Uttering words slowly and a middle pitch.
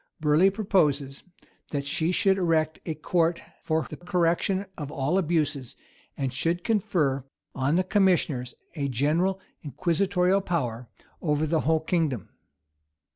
Yes: slow, 130 wpm; medium, 160 Hz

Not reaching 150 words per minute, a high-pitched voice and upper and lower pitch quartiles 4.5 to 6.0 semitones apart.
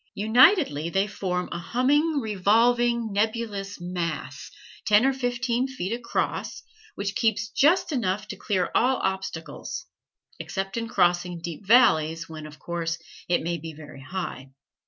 Yes: average, 140 wpm; high, 200 Hz; wide, 5.6 semitones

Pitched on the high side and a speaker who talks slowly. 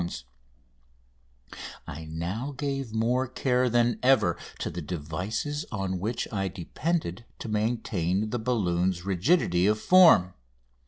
No: low, 105 Hz; slow, 125 wpm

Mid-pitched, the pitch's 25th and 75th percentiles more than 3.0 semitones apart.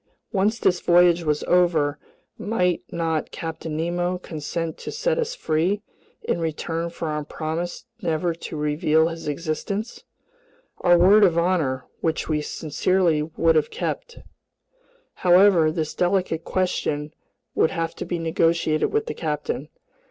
No: medium, 165 Hz; narrow, 2.4 semitones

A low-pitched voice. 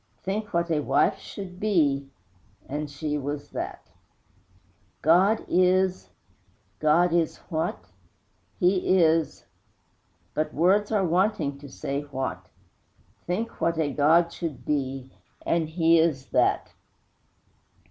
No: medium, 165 Hz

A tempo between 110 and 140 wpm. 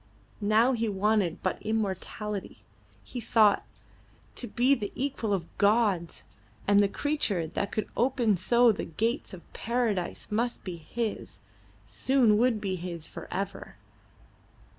Yes: slow, 135 wpm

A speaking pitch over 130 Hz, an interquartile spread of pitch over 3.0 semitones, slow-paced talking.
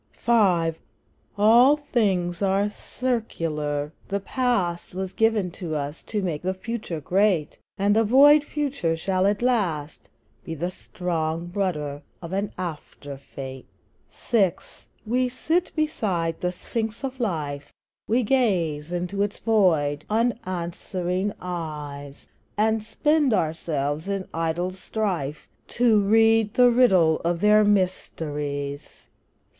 Yes: medium, 185 Hz; wide, 5.4 semitones; slow, 120 wpm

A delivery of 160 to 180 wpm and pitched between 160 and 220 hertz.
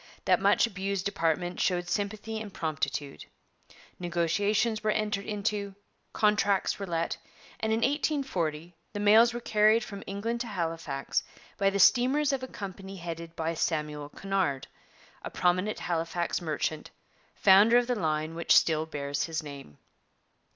No: average, 145 wpm; high, 190 Hz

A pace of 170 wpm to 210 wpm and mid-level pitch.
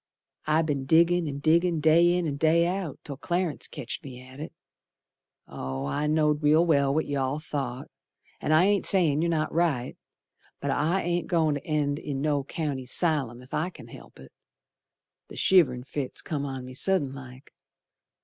Yes: average, 180 wpm; medium, 150 Hz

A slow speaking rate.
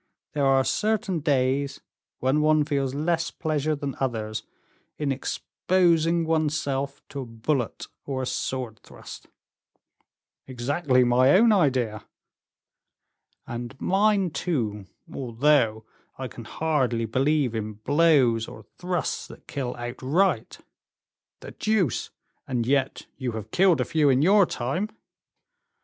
Yes: slow, 125 wpm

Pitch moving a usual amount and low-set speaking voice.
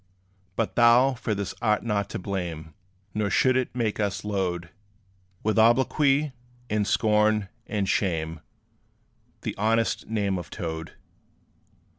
Yes: average, 3.3 semitones; low, 105 Hz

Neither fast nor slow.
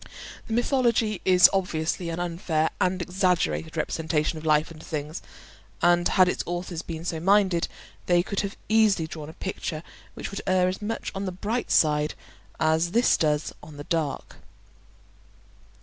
Yes: average, 160 wpm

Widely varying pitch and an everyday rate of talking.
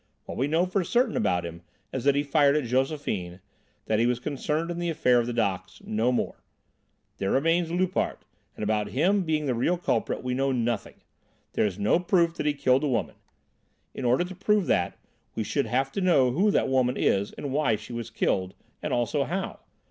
No: wide, 6.0 semitones; fast, 210 wpm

